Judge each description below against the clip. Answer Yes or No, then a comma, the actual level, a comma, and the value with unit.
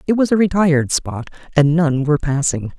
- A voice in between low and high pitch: Yes, medium, 160 Hz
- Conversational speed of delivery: Yes, average, 195 wpm